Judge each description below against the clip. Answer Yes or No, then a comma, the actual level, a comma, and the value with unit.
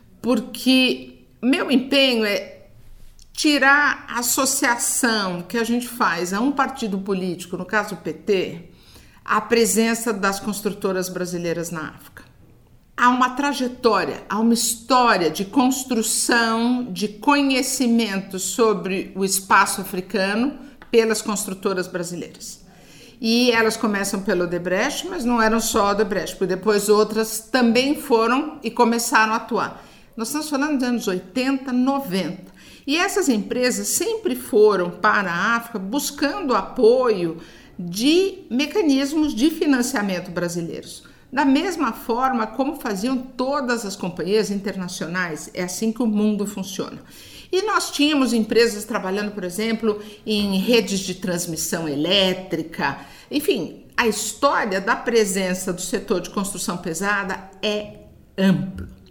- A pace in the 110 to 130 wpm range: Yes, average, 125 wpm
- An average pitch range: Yes, average, 4.9 semitones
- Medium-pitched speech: No, high, 220 Hz